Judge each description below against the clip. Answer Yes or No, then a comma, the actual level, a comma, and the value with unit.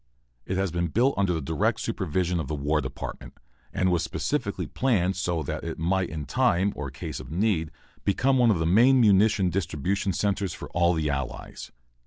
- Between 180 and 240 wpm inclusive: Yes, average, 190 wpm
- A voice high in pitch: No, very low, 90 Hz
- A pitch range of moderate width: Yes, average, 3.8 semitones